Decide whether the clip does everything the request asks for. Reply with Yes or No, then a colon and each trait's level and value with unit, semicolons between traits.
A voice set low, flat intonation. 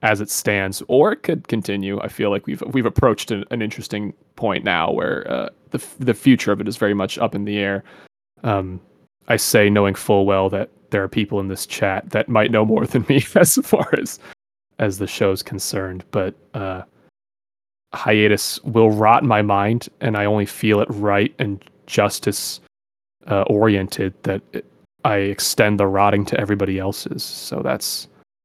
Yes: low, 105 Hz; narrow, 2.0 semitones